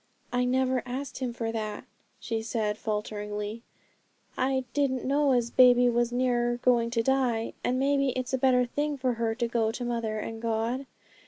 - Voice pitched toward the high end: Yes, high, 245 Hz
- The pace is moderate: Yes, average, 175 wpm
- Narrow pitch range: Yes, narrow, 2.3 semitones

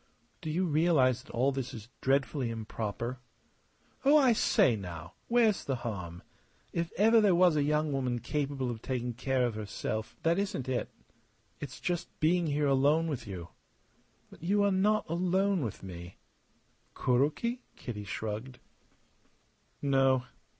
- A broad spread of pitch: Yes, wide, 6.6 semitones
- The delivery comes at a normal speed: Yes, average, 150 wpm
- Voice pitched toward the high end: No, low, 135 Hz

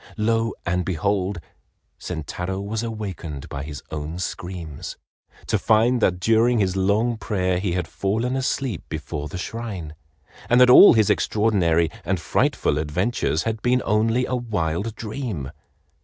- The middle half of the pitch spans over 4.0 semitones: Yes, average, 5.0 semitones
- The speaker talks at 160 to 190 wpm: No, average, 140 wpm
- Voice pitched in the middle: No, low, 100 Hz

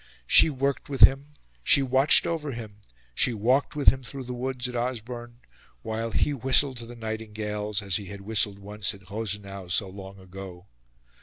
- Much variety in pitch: No, average, 4.3 semitones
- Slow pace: No, average, 175 wpm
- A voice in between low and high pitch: No, low, 110 Hz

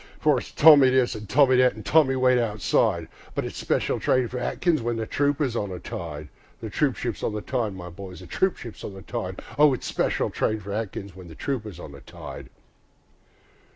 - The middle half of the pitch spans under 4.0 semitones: No, average, 5.3 semitones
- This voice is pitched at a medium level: No, low, 115 Hz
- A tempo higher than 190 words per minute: Yes, fast, 205 wpm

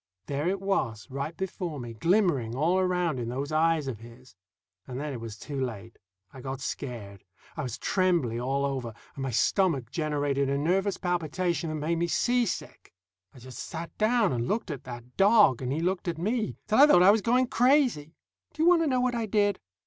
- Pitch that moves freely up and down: Yes, wide, 6.9 semitones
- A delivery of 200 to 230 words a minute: Yes, fast, 205 wpm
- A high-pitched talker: No, medium, 155 Hz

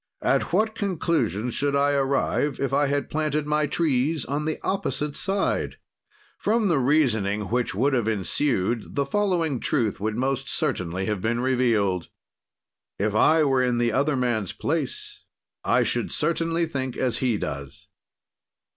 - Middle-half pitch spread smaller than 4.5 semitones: No, average, 5.2 semitones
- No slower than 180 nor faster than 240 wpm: No, average, 150 wpm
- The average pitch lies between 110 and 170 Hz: Yes, low, 135 Hz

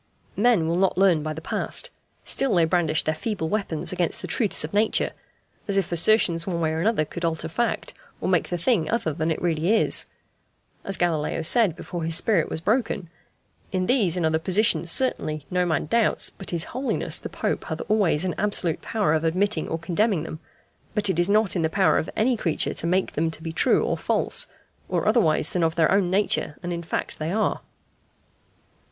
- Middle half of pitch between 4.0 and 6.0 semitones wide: Yes, average, 4.3 semitones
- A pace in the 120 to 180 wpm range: No, fast, 205 wpm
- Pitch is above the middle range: No, medium, 175 Hz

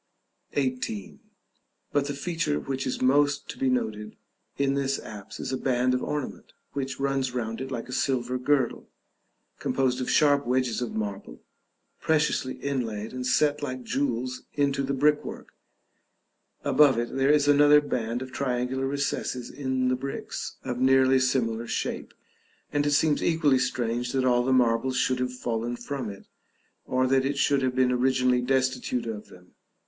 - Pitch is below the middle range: Yes, low, 130 Hz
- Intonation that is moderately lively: No, narrow, 2.0 semitones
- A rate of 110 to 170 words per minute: Yes, average, 165 wpm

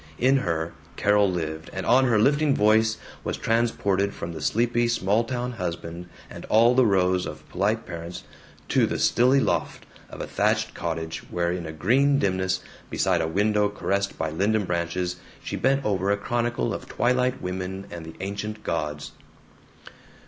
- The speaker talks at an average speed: Yes, average, 165 wpm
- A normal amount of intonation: Yes, average, 5.0 semitones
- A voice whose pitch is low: Yes, low, 100 Hz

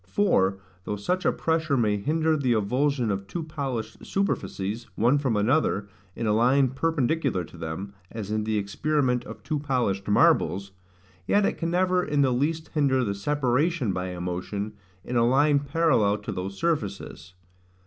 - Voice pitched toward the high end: No, low, 125 Hz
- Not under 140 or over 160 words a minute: No, average, 170 wpm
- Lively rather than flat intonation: Yes, wide, 6.7 semitones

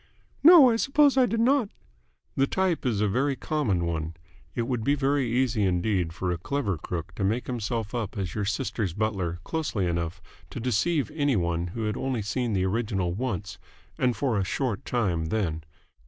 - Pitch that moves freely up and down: Yes, wide, 6.5 semitones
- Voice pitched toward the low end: Yes, low, 110 Hz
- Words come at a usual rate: Yes, average, 185 wpm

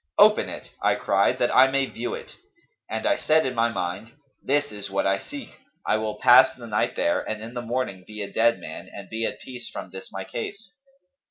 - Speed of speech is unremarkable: No, fast, 225 wpm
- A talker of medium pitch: No, low, 115 Hz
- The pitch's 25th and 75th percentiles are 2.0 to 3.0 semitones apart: No, average, 4.1 semitones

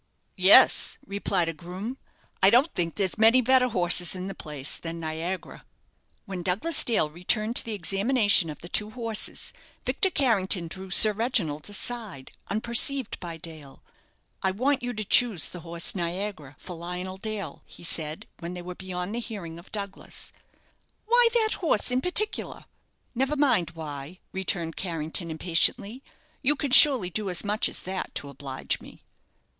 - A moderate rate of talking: Yes, average, 160 wpm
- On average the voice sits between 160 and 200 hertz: Yes, high, 190 Hz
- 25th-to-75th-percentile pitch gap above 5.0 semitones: Yes, wide, 5.4 semitones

